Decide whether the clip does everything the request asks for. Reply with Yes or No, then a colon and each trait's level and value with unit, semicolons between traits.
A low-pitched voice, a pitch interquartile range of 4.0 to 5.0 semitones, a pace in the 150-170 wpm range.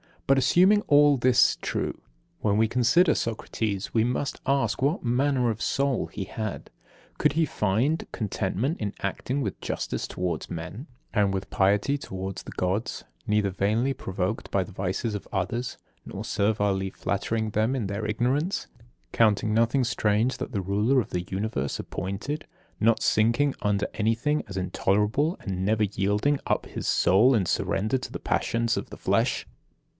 Yes: low, 110 Hz; average, 4.7 semitones; average, 160 wpm